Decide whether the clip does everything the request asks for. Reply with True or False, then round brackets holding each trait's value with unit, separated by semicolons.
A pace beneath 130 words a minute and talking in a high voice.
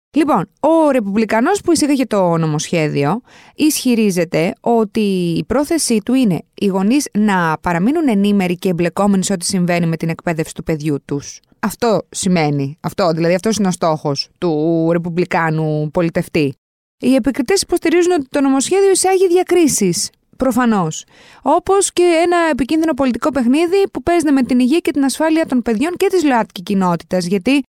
False (150 wpm; 220 Hz)